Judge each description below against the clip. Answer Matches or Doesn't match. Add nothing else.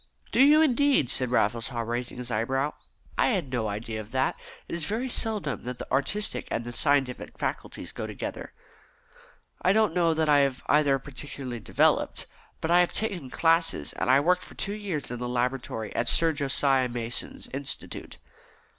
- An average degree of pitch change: Doesn't match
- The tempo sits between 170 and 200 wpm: Matches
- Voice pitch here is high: Doesn't match